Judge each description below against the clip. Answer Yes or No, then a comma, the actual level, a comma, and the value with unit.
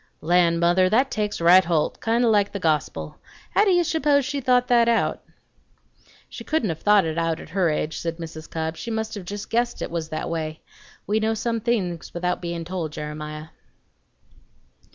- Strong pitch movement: Yes, wide, 5.8 semitones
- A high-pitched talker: No, medium, 180 Hz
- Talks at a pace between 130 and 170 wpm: No, average, 195 wpm